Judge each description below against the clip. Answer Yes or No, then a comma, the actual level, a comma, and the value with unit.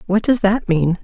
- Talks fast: Yes, fast, 235 wpm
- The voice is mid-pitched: No, high, 195 Hz